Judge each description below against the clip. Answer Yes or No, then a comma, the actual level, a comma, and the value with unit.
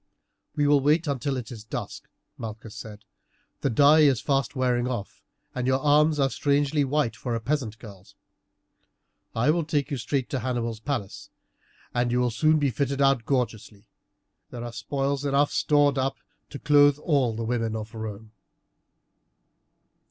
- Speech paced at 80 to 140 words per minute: No, average, 160 wpm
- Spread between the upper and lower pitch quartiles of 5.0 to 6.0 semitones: No, average, 4.0 semitones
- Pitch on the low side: Yes, low, 130 Hz